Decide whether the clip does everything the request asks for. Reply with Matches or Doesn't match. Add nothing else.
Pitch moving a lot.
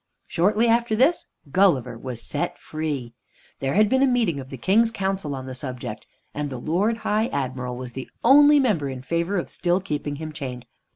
Matches